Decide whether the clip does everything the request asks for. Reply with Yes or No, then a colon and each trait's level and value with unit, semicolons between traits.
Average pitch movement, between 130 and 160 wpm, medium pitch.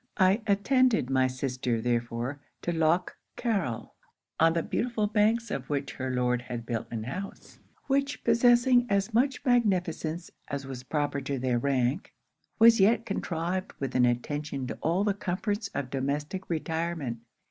No: wide, 7.9 semitones; average, 150 wpm; medium, 160 Hz